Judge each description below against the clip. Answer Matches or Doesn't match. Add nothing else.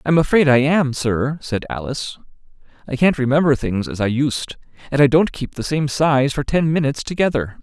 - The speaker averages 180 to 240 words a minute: Matches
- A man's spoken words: Matches